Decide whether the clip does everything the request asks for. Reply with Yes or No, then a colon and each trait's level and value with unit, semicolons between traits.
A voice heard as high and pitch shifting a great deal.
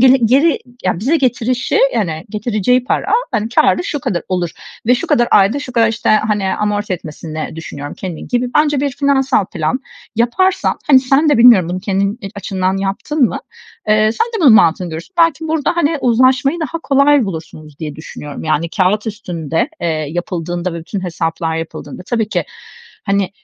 Yes: high, 215 Hz; wide, 7.0 semitones